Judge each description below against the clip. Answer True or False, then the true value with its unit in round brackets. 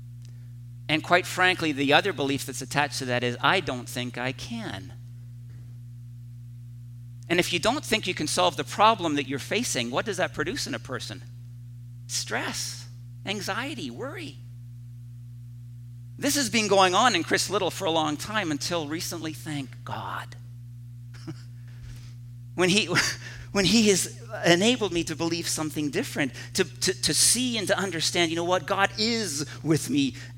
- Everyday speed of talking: True (155 wpm)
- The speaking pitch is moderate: False (125 Hz)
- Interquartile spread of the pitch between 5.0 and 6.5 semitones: True (5.6 semitones)